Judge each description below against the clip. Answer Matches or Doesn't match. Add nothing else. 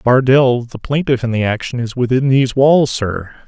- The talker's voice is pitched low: Matches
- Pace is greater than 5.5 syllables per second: Doesn't match